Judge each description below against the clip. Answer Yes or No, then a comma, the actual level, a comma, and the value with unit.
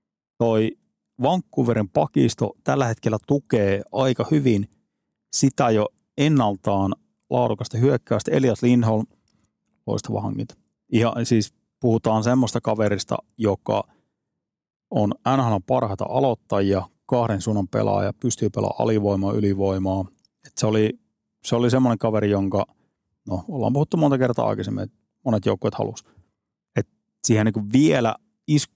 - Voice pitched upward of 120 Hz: No, low, 115 Hz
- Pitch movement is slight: No, average, 3.5 semitones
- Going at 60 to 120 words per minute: Yes, average, 115 wpm